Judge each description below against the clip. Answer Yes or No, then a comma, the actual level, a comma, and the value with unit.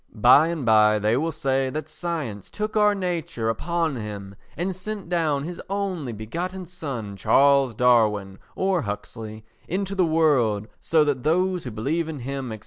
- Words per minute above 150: Yes, average, 165 wpm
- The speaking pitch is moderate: Yes, medium, 145 Hz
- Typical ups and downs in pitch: No, wide, 7.4 semitones